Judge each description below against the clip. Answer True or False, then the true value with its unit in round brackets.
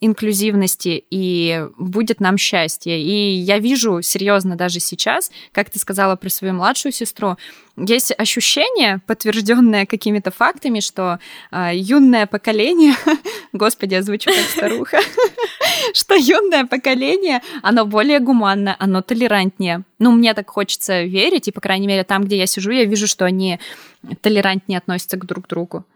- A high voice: True (205 Hz)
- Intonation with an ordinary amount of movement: True (4.0 semitones)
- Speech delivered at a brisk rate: False (145 wpm)